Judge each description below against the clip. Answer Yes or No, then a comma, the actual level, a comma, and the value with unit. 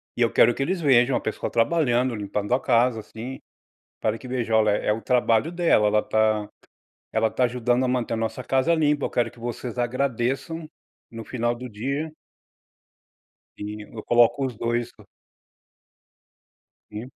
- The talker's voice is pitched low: Yes, low, 120 Hz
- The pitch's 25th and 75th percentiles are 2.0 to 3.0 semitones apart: Yes, average, 2.7 semitones